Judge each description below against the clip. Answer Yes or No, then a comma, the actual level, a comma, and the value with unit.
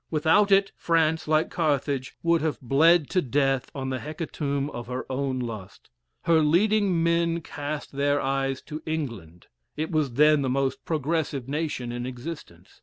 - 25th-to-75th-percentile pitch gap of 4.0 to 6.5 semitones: No, average, 3.5 semitones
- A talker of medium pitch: Yes, medium, 145 Hz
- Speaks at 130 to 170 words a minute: Yes, average, 160 wpm